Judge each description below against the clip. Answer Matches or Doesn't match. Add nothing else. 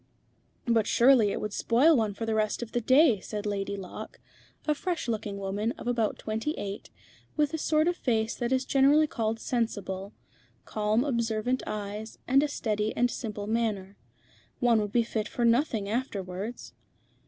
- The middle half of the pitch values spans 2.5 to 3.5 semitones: Matches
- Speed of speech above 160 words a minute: Matches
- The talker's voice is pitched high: Matches